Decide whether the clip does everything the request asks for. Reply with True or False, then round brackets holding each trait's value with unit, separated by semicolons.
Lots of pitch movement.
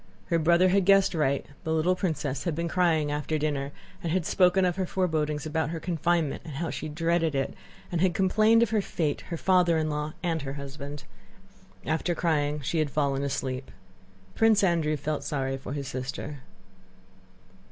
False (3.2 semitones)